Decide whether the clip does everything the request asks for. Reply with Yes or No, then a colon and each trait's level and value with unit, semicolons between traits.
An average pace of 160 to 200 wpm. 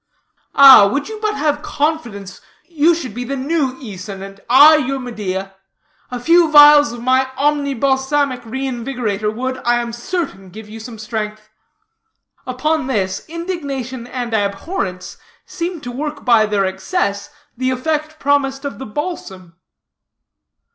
No: average, 140 wpm